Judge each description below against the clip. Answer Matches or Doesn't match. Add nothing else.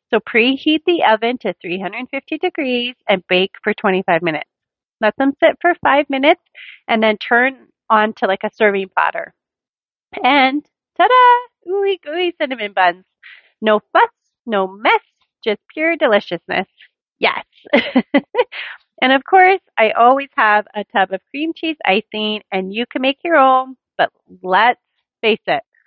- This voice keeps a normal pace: Matches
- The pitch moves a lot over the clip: Matches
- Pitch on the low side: Doesn't match